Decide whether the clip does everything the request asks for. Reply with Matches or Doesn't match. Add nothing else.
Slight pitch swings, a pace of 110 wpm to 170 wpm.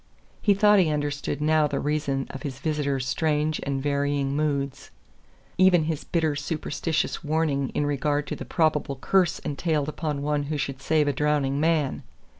Matches